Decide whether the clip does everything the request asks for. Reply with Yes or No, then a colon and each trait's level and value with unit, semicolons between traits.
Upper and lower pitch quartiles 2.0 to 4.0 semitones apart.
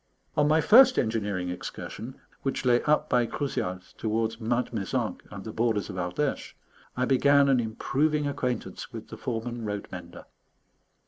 No: average, 4.9 semitones